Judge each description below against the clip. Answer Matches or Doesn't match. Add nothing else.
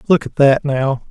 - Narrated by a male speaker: Matches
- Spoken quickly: Matches